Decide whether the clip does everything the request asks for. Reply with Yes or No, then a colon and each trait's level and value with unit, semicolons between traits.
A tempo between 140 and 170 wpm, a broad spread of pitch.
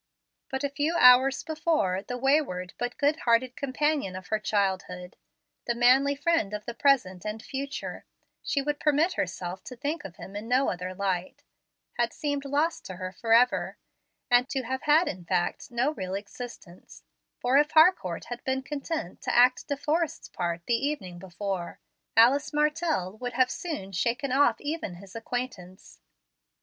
Yes: average, 160 wpm; wide, 7.0 semitones